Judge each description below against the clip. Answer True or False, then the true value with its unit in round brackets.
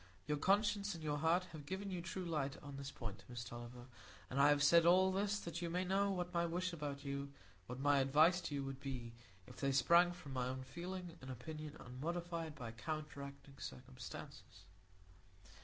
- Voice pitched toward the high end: False (150 Hz)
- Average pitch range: True (4.5 semitones)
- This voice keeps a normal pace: True (185 wpm)